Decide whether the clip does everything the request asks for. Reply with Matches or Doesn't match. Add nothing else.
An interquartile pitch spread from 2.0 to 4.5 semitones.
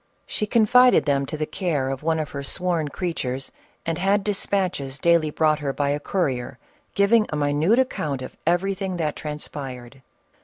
Doesn't match